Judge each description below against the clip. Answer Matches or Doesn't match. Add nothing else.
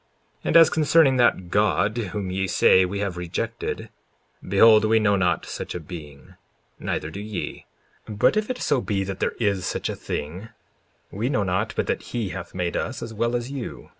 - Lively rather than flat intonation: Doesn't match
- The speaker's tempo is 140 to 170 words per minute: Doesn't match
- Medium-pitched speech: Doesn't match